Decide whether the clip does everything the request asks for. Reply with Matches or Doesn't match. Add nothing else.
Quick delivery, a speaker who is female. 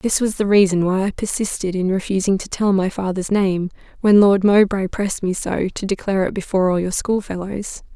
Matches